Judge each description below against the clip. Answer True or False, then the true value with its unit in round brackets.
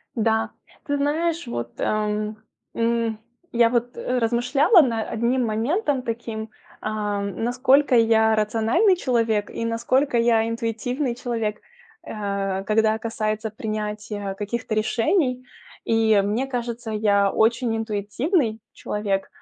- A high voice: True (225 Hz)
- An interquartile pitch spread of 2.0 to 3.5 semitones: True (2.4 semitones)